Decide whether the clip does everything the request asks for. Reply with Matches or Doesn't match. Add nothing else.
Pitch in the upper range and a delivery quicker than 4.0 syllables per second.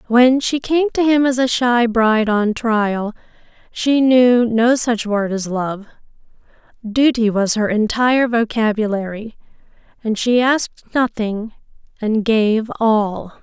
Doesn't match